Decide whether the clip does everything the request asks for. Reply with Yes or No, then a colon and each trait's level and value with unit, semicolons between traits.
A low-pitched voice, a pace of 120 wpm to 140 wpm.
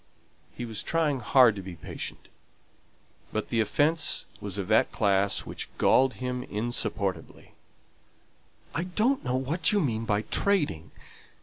Yes: low, 120 Hz; slow, 135 wpm